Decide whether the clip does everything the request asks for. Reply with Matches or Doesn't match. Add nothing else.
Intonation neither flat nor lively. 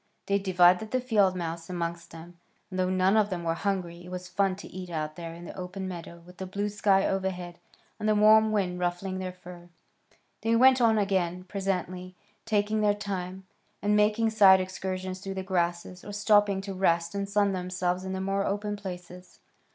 Doesn't match